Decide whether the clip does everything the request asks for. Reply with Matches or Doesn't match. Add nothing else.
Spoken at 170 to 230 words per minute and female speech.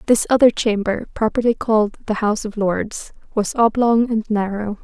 Doesn't match